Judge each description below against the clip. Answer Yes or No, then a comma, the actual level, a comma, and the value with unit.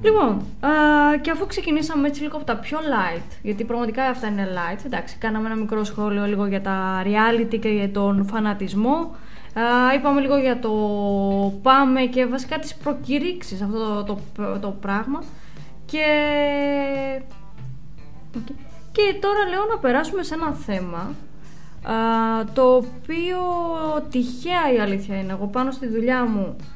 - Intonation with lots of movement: Yes, wide, 6.4 semitones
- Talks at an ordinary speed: Yes, average, 150 wpm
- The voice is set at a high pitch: Yes, high, 240 Hz